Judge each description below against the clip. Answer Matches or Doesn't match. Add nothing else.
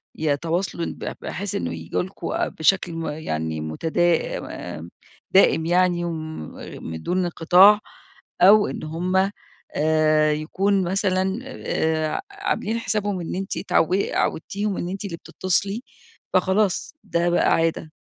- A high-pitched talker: Doesn't match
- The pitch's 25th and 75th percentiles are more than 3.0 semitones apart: Matches